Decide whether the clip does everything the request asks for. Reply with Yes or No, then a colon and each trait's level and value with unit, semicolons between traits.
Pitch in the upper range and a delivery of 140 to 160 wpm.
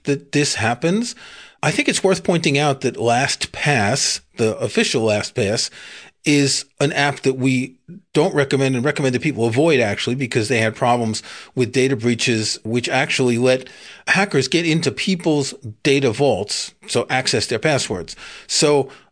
No: low, 135 Hz; average, 150 wpm